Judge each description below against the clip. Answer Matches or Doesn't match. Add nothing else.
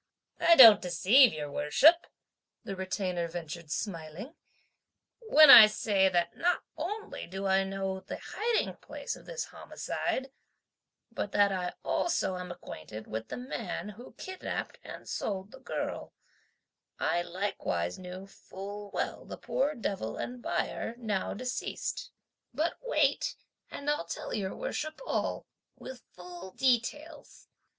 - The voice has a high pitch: Matches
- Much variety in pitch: Matches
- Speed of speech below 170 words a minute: Matches